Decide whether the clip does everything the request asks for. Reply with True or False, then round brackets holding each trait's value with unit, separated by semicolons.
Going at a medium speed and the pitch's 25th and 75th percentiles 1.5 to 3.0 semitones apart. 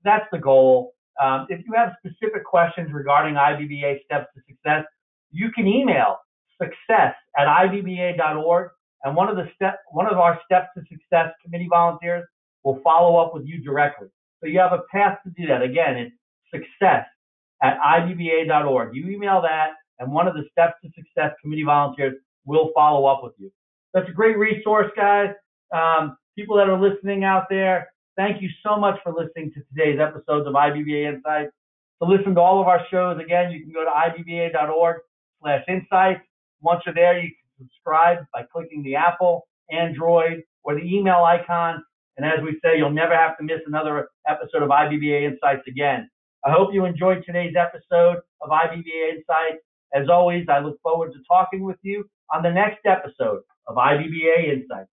False (180 wpm; 3.5 semitones)